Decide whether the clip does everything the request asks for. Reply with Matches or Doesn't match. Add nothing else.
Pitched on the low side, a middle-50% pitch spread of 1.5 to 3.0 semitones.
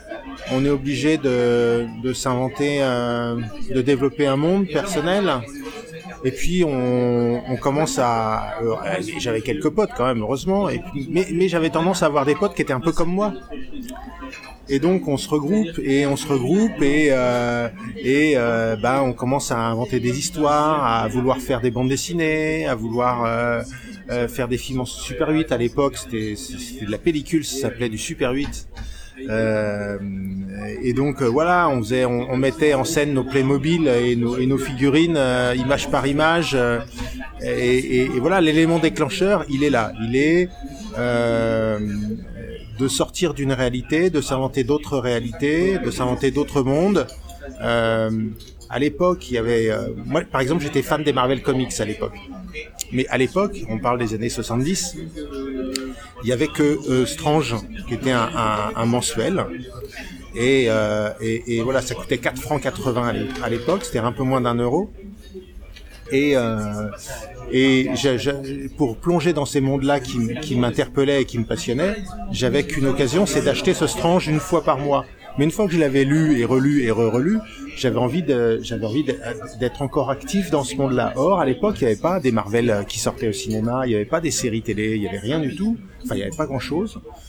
Doesn't match